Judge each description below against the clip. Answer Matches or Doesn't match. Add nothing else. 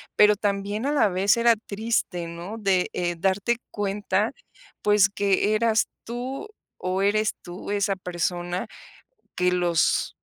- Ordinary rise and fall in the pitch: Matches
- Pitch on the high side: Matches